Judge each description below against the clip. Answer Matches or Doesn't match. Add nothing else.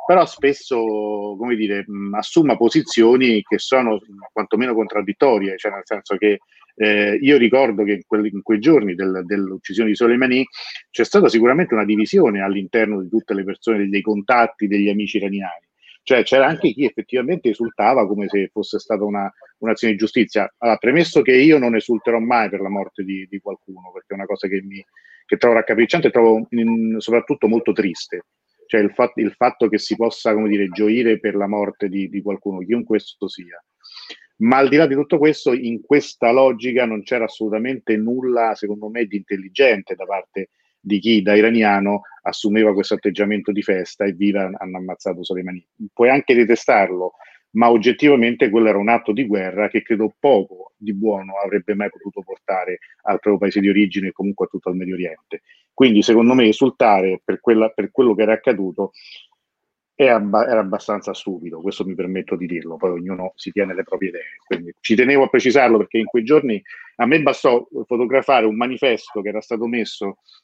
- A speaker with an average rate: Doesn't match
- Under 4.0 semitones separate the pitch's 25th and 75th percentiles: Matches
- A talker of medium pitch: Doesn't match